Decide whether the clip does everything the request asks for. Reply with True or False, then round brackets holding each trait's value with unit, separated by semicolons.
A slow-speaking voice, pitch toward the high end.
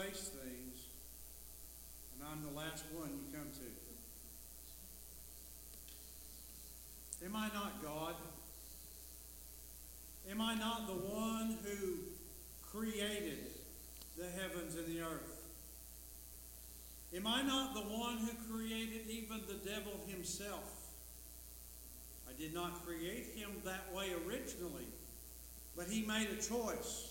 False (110 wpm; 155 Hz)